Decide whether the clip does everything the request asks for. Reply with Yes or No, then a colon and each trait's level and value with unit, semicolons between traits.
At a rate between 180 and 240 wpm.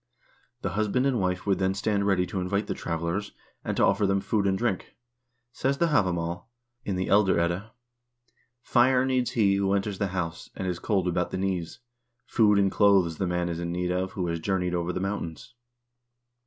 Yes: average, 195 wpm